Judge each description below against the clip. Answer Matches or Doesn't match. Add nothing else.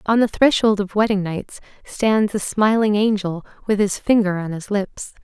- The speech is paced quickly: Doesn't match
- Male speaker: Doesn't match